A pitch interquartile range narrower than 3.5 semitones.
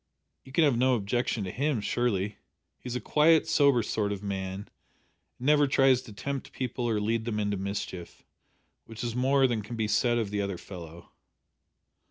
No: average, 4.2 semitones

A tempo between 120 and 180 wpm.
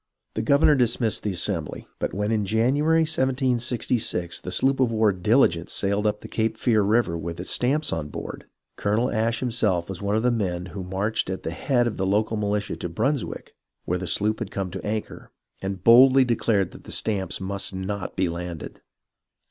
No: average, 195 wpm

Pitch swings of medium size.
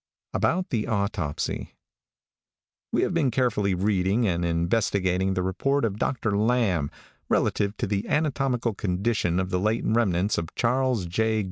Yes: average, 4.2 semitones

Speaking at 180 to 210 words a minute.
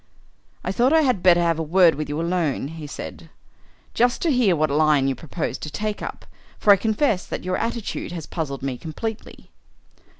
Yes: average, 195 wpm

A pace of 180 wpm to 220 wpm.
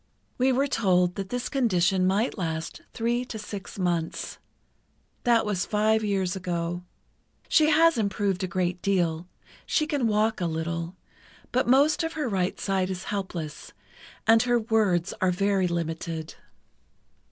No: average, 145 wpm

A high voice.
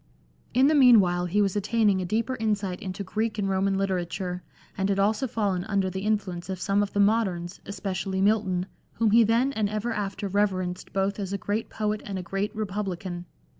Yes: high, 200 Hz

